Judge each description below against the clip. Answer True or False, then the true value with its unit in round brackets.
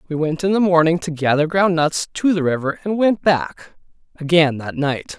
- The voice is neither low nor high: True (165 Hz)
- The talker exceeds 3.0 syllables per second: True (4.9 syllables/s)